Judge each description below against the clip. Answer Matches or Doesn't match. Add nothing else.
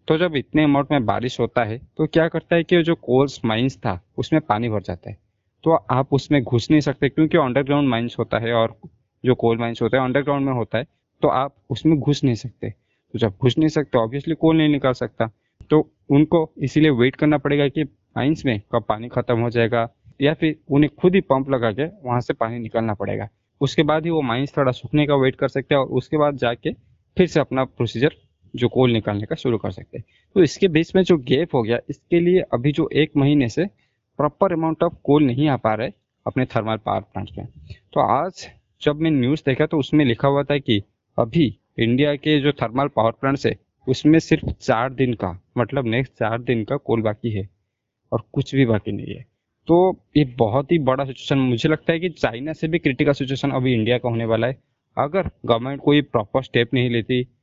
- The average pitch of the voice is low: Matches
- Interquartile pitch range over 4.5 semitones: Doesn't match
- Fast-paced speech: Matches